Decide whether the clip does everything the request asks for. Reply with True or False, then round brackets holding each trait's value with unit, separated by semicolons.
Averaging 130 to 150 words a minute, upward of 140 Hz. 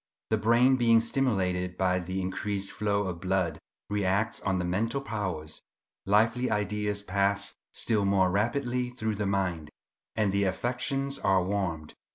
False (145 wpm; 100 Hz)